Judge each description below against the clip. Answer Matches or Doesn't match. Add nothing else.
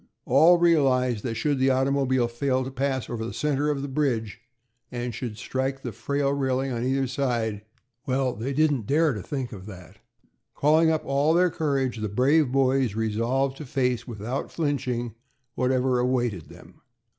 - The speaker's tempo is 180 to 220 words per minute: Doesn't match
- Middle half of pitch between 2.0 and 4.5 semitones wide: Matches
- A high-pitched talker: Doesn't match